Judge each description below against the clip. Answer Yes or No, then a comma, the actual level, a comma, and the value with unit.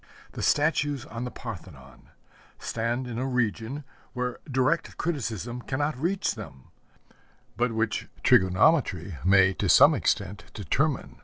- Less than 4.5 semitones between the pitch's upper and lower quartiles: No, average, 5.3 semitones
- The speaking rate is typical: No, slow, 125 wpm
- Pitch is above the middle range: No, low, 120 Hz